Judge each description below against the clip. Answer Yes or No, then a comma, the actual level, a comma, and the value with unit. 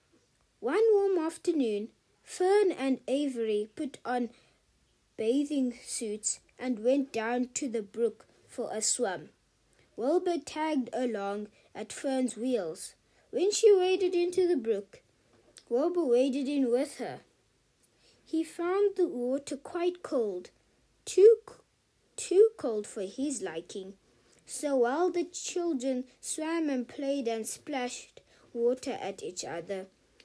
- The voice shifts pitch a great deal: Yes, wide, 6.8 semitones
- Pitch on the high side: Yes, very high, 275 Hz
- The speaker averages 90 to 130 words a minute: Yes, slow, 120 wpm